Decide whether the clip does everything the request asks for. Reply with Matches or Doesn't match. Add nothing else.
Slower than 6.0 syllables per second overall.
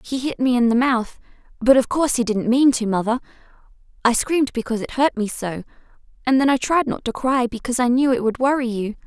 Doesn't match